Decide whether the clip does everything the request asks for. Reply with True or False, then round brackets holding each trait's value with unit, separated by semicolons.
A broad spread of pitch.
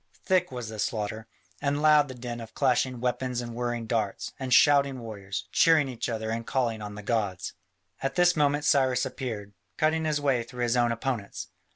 False (3.7 semitones)